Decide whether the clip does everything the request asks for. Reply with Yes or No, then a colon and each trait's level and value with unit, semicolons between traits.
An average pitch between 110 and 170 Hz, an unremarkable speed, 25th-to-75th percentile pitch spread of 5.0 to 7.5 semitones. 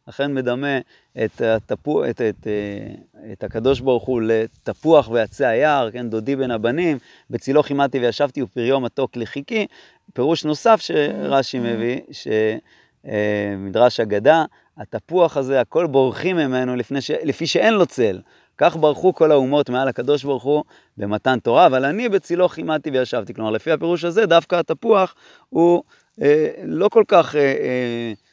Yes: low, 135 Hz; average, 140 wpm; average, 5.3 semitones